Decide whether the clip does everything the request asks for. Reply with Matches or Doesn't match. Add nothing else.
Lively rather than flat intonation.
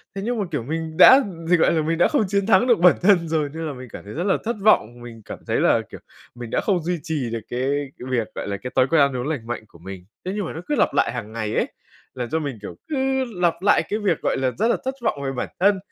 Matches